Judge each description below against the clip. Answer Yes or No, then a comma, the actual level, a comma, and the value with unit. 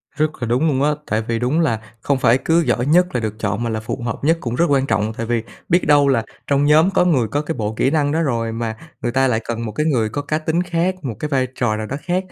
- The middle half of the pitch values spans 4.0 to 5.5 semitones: Yes, average, 5.1 semitones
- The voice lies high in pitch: No, low, 130 Hz